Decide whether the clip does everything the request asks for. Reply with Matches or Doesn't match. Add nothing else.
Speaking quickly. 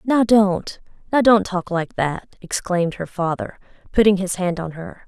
Doesn't match